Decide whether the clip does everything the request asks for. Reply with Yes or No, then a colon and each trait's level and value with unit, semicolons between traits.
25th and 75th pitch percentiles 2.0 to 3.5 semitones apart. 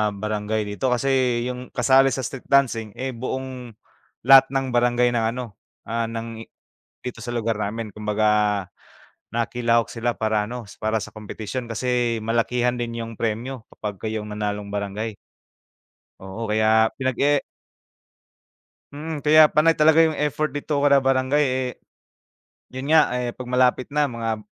Yes: average, 3.1 semitones